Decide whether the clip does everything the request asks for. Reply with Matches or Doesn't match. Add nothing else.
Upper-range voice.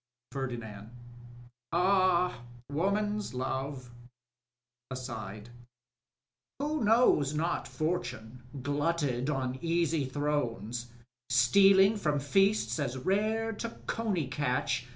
Doesn't match